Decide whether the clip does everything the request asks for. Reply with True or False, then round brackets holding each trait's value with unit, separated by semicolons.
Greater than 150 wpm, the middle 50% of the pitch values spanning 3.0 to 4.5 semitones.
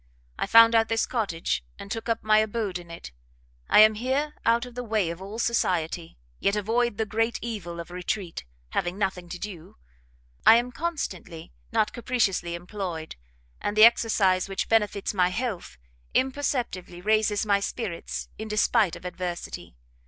True (160 wpm; 4.1 semitones)